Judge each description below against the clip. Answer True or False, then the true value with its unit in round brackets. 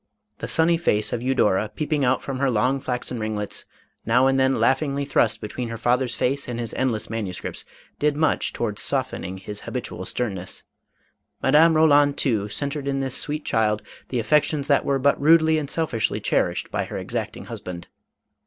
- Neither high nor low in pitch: False (130 Hz)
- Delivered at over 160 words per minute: True (180 wpm)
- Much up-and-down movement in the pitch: False (4.2 semitones)